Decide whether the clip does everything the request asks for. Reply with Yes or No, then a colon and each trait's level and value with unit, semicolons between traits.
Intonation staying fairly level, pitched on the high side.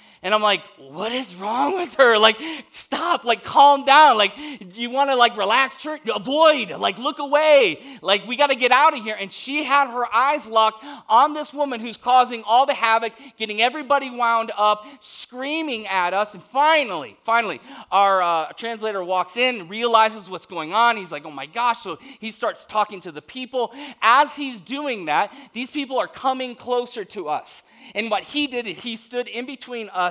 No: average, 4.7 semitones; high, 245 Hz